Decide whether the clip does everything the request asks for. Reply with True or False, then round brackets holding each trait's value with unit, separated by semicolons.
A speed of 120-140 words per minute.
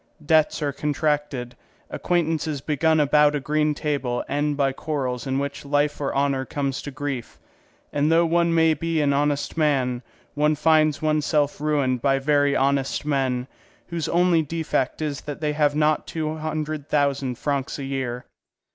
False (160 wpm)